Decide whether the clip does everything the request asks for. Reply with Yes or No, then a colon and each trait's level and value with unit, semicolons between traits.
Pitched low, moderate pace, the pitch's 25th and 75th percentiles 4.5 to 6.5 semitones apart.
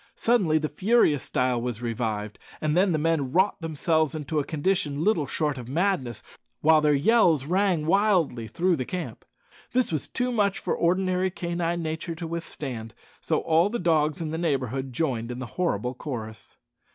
No: medium, 155 Hz; average, 170 wpm; average, 5.3 semitones